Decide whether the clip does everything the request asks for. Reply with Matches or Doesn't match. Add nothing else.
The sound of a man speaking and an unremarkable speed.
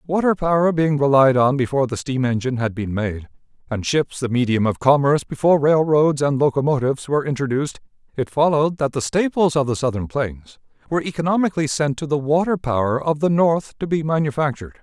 Matches